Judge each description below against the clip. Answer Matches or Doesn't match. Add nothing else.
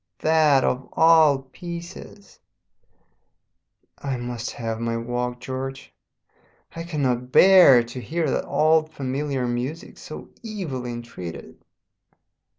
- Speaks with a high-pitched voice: Doesn't match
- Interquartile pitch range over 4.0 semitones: Matches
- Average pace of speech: Doesn't match